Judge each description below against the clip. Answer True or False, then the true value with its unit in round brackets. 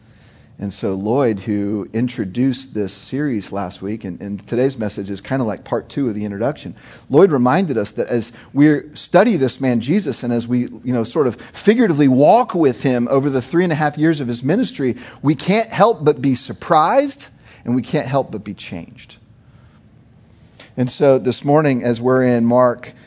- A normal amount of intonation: True (3.6 semitones)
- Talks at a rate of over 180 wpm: True (190 wpm)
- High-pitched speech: False (125 Hz)